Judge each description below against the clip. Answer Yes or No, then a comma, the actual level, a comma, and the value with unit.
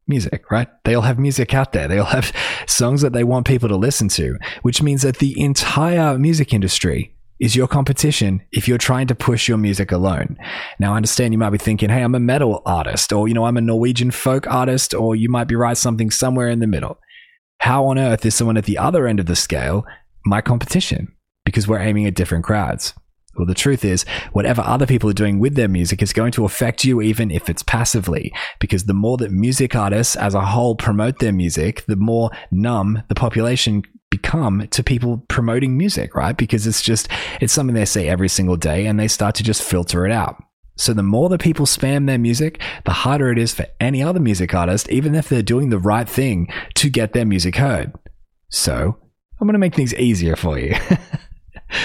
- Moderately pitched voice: No, low, 115 Hz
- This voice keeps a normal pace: No, fast, 215 wpm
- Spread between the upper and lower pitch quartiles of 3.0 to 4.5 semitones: Yes, average, 4.0 semitones